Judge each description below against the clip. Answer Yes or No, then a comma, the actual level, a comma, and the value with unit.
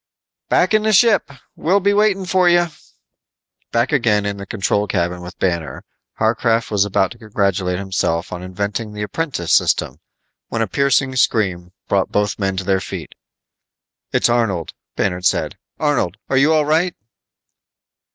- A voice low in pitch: Yes, low, 105 Hz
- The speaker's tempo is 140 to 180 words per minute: Yes, average, 150 wpm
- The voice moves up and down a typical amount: No, wide, 7.5 semitones